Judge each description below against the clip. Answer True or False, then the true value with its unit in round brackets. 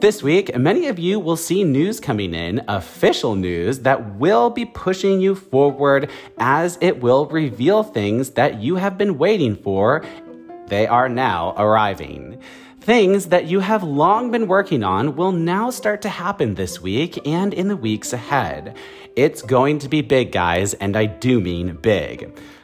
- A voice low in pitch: False (145 Hz)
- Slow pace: False (170 wpm)